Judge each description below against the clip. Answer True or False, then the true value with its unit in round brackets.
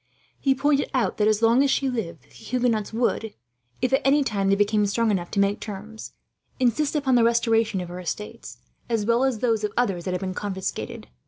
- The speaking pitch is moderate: False (225 Hz)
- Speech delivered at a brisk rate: True (215 wpm)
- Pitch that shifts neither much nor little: True (3.9 semitones)